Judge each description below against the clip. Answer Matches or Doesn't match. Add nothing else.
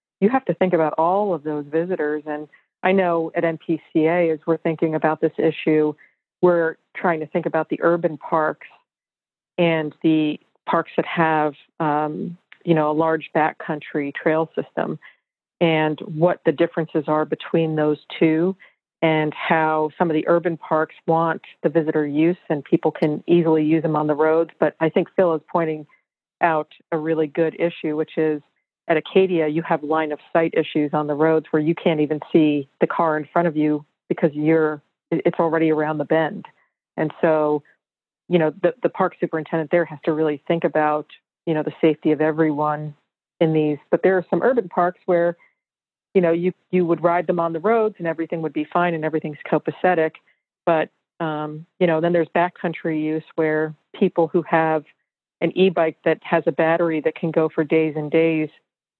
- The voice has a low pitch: Doesn't match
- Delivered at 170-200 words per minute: Matches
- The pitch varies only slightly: Matches